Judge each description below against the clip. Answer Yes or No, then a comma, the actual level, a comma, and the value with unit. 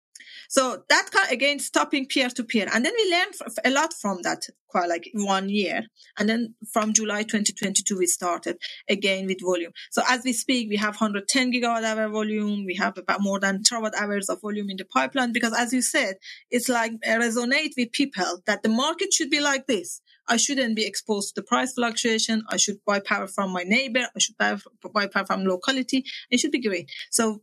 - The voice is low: No, high, 225 Hz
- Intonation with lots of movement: No, average, 4.2 semitones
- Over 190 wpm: Yes, fast, 205 wpm